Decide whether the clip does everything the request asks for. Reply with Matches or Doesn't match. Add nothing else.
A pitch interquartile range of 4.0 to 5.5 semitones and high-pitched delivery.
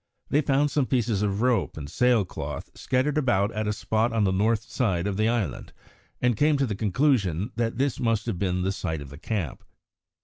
Doesn't match